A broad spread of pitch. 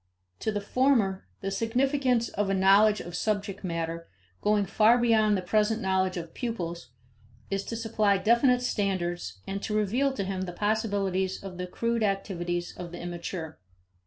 No: average, 3.4 semitones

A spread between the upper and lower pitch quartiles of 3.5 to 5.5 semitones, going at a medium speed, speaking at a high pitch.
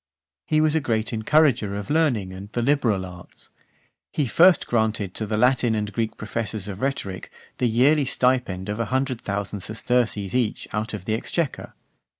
No: average, 4.1 semitones; average, 175 wpm; low, 110 Hz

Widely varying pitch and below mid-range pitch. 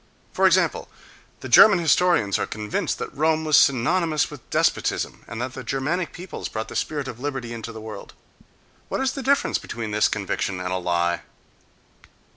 Yes: wide, 6.9 semitones; low, 130 Hz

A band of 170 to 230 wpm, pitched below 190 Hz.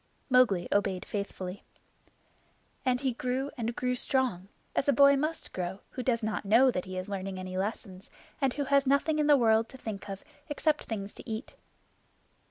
No: average, 180 wpm; high, 230 Hz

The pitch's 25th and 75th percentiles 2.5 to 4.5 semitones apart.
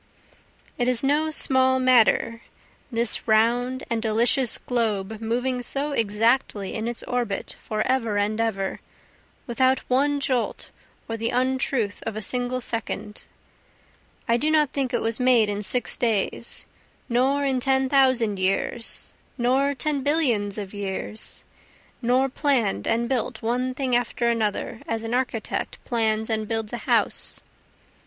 Yes: average, 2.9 semitones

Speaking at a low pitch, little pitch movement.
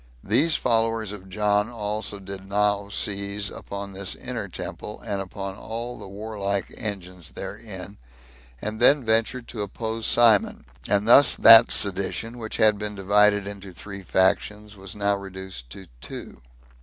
Yes: low, 105 Hz; narrow, 2.1 semitones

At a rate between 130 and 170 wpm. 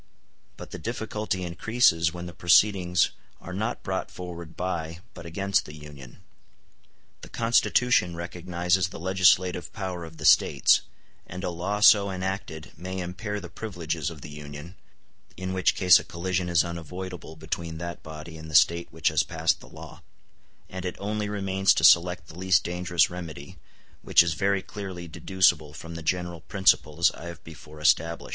Yes: average, 165 wpm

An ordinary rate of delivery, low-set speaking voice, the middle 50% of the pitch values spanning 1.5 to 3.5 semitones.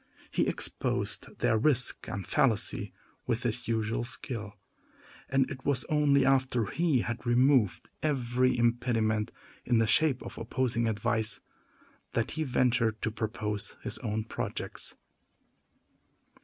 No: slow, 125 wpm; low, 120 Hz; average, 3.0 semitones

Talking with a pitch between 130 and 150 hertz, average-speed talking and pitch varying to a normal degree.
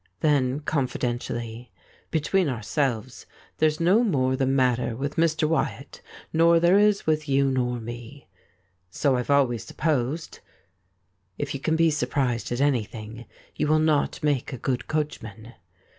Yes: medium, 140 Hz; average, 145 wpm; average, 4.2 semitones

